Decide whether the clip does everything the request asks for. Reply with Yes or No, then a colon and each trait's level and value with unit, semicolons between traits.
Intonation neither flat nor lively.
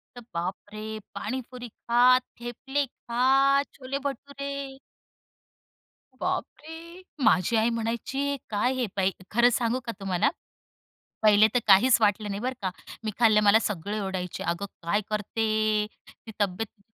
Yes: average, 4.1 semitones